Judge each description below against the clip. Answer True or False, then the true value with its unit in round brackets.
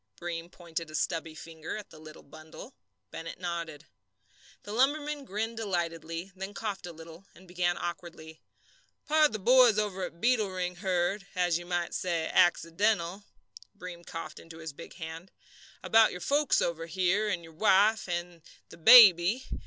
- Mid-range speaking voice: True (175 Hz)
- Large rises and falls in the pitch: False (3.8 semitones)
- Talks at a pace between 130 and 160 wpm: True (155 wpm)